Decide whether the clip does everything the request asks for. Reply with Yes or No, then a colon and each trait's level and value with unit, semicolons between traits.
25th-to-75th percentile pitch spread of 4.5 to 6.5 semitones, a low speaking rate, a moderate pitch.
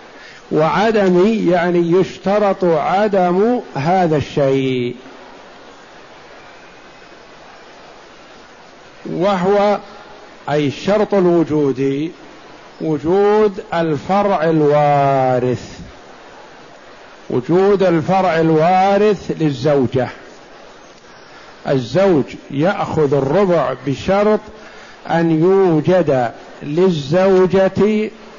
Yes: average, 5.1 semitones; slow, 50 wpm; medium, 175 Hz